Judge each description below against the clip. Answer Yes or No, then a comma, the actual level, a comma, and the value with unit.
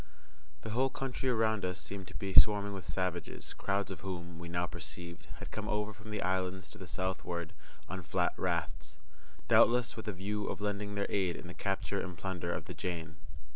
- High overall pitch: No, very low, 95 Hz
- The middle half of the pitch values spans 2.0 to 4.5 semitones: Yes, average, 3.0 semitones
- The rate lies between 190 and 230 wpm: Yes, average, 200 wpm